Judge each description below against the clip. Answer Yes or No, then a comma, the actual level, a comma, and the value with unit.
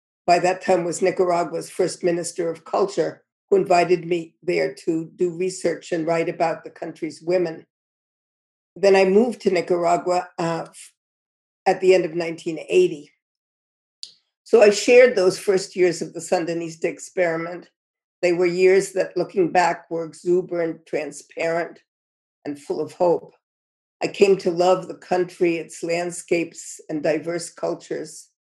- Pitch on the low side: No, medium, 175 Hz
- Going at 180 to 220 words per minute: No, average, 140 wpm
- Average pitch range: No, narrow, 1.7 semitones